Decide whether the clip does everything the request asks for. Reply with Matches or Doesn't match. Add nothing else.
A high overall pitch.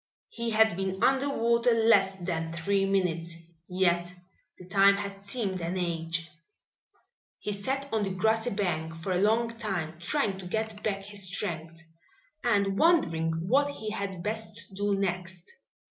Matches